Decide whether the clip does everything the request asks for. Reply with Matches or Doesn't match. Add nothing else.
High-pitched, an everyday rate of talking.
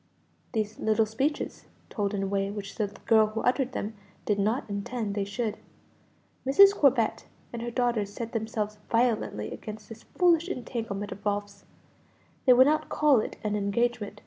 Matches